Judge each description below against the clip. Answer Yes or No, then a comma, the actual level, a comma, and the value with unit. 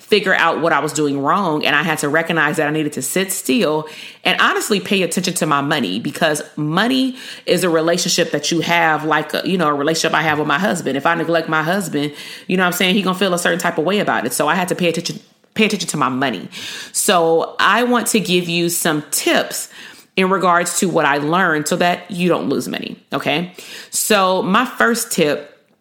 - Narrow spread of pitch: No, average, 3.5 semitones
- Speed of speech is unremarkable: No, fast, 235 wpm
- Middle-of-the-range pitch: Yes, medium, 170 Hz